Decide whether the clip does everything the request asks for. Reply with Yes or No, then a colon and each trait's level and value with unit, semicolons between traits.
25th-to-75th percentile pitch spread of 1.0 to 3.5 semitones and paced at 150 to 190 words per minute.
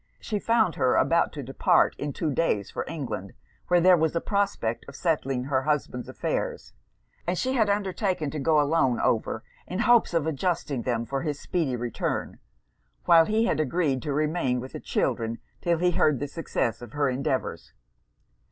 No: average, 5.1 semitones; average, 180 wpm